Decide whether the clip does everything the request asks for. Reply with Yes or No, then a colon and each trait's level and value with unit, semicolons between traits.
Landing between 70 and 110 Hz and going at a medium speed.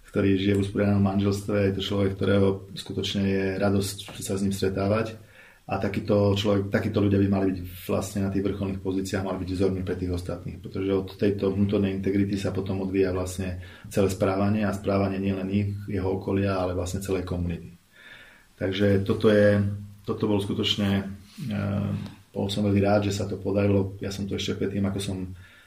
No: low, 100 Hz; fast, 180 wpm